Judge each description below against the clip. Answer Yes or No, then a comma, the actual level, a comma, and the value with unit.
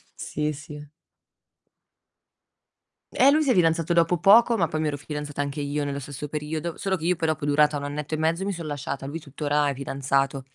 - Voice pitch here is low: No, medium, 150 Hz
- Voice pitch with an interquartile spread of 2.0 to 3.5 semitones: Yes, narrow, 2.5 semitones